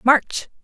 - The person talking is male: No, female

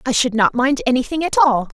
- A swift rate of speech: Yes, fast, 235 wpm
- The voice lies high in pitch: Yes, high, 245 Hz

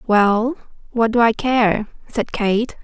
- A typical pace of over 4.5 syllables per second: No, 3.4 syllables/s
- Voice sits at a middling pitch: No, high, 225 Hz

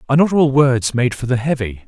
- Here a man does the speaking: Yes, male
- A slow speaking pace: No, fast, 255 wpm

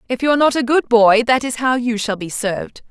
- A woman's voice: Yes, female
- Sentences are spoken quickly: Yes, fast, 270 wpm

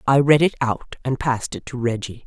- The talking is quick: Yes, fast, 240 wpm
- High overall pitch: No, low, 130 Hz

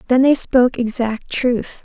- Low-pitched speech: No, high, 245 Hz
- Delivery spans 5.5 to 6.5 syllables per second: No, 4.3 syllables/s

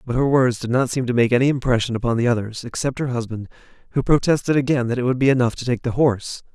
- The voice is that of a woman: No, male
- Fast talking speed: Yes, fast, 255 wpm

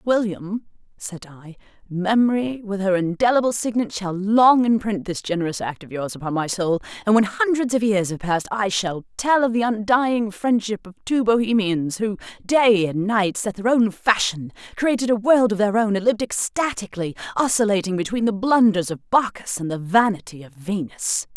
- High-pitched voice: Yes, high, 210 Hz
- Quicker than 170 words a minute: Yes, average, 180 wpm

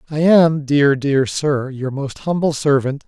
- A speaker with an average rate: Yes, average, 175 wpm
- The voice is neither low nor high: Yes, medium, 145 Hz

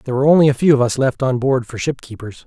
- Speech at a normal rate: No, fast, 315 wpm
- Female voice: No, male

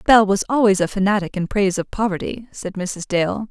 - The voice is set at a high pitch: Yes, high, 200 Hz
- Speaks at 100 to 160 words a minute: No, fast, 205 wpm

